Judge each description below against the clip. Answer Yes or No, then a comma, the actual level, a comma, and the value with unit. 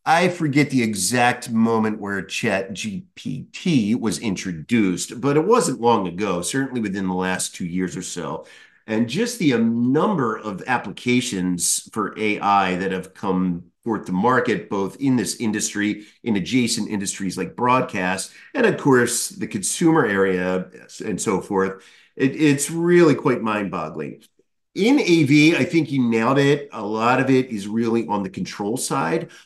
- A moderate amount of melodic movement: No, wide, 5.9 semitones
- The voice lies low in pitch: Yes, low, 115 Hz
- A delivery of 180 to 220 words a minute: No, average, 160 wpm